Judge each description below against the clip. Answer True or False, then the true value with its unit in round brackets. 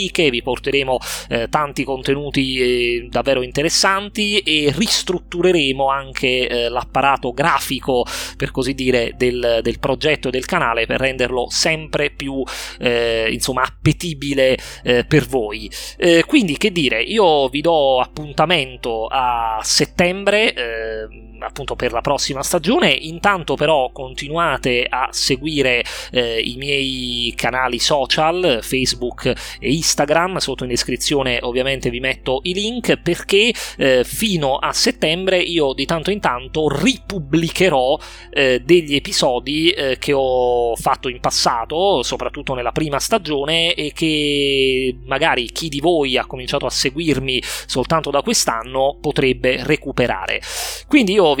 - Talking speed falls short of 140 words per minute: True (130 wpm)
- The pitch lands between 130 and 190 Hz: True (135 Hz)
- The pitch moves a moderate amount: True (4.2 semitones)